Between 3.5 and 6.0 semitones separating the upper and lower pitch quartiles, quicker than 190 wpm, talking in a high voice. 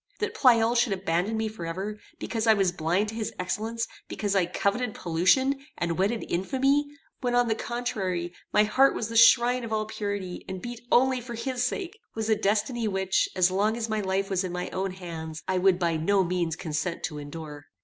Yes: average, 4.6 semitones; average, 200 wpm; high, 205 Hz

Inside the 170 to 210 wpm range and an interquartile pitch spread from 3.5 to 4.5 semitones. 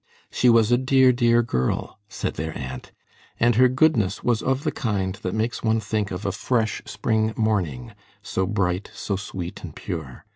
Yes: average, 180 wpm; average, 4.2 semitones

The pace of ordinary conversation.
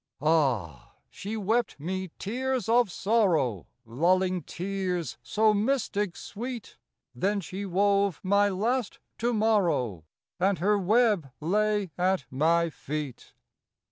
No: slow, 110 wpm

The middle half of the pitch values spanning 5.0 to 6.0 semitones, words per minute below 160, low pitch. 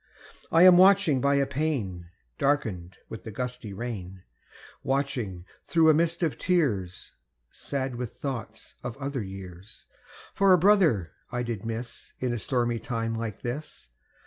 Yes: wide, 5.6 semitones; average, 145 wpm; low, 125 Hz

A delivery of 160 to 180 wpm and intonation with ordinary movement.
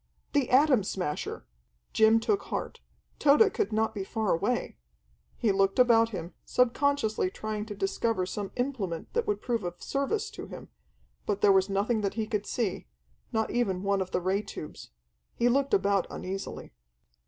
Yes: average, 165 wpm; average, 4.2 semitones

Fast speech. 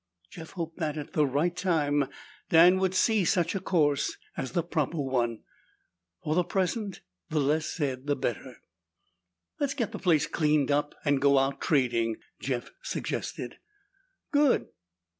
No: average, 150 wpm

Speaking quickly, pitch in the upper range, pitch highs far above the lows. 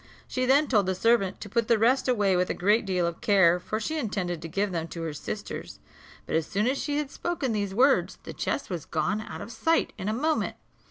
Yes: fast, 240 wpm; high, 210 Hz; wide, 5.8 semitones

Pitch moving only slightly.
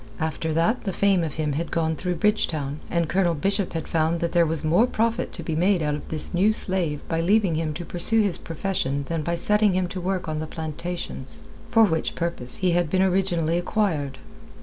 No: average, 3.2 semitones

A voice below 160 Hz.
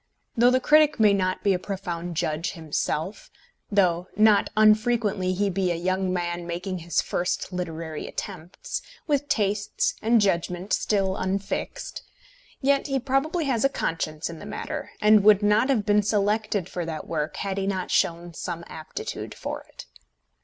No: high, 195 Hz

